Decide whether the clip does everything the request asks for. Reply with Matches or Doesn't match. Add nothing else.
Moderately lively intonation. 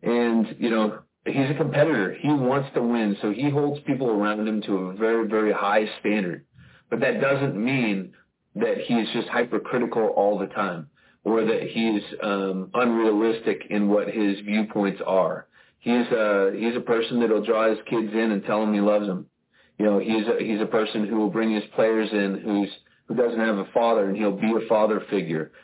Doesn't match